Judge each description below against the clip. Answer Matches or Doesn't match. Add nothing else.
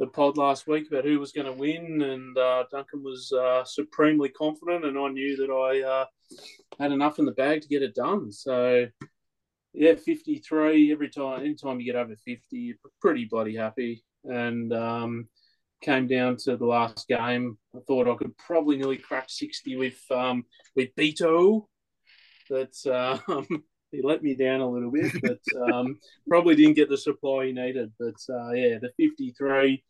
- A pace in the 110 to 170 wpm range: Doesn't match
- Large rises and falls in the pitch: Doesn't match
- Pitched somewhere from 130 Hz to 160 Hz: Matches